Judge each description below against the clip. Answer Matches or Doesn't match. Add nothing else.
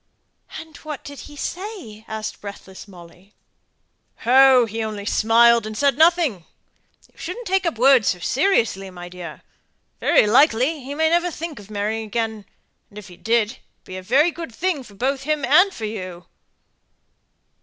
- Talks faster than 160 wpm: Matches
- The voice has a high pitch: Matches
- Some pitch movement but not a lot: Doesn't match